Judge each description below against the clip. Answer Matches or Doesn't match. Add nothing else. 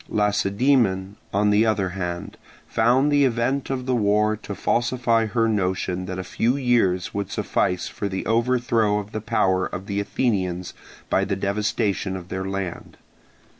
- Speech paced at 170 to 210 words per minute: Doesn't match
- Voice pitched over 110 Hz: Doesn't match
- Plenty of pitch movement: Doesn't match